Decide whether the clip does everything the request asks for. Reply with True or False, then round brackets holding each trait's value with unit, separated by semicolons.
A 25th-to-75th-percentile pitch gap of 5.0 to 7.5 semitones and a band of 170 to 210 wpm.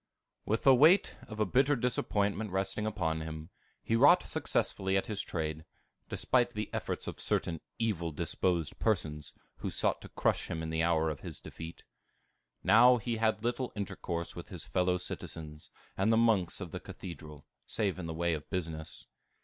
True (5.5 semitones; 175 wpm)